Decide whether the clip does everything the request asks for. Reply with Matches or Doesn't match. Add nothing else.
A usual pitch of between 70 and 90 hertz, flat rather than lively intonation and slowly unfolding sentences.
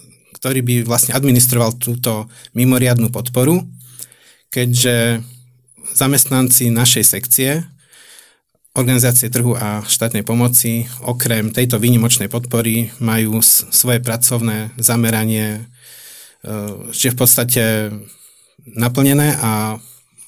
Doesn't match